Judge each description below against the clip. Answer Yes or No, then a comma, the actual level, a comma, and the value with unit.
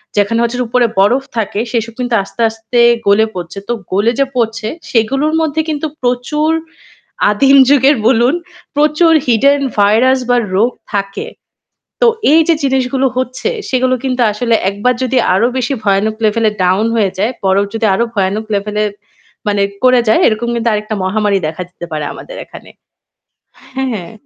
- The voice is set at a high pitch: Yes, high, 230 Hz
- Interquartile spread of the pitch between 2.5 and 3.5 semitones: No, average, 3.9 semitones